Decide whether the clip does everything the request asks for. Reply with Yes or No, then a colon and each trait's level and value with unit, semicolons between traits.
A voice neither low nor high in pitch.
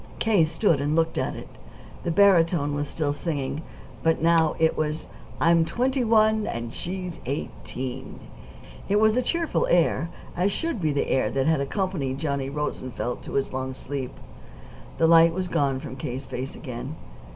Yes: medium, 160 Hz